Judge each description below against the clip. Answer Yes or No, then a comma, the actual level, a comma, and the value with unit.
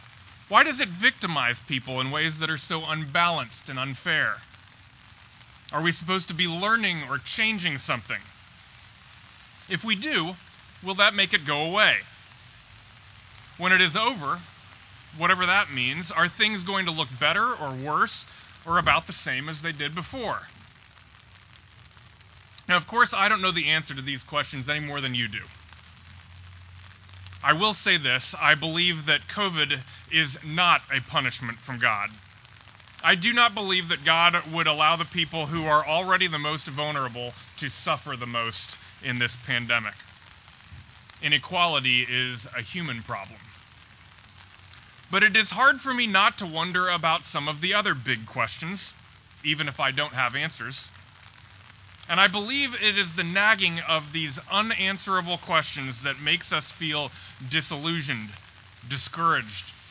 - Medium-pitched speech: Yes, medium, 145 Hz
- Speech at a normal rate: Yes, average, 150 wpm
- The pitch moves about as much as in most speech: No, wide, 7.5 semitones